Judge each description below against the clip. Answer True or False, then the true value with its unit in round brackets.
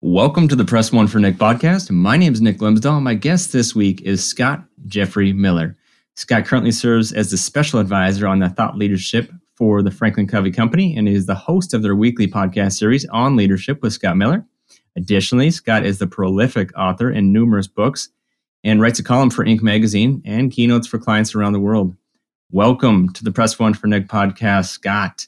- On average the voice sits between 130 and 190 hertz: False (110 Hz)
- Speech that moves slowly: False (195 wpm)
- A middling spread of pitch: True (3.2 semitones)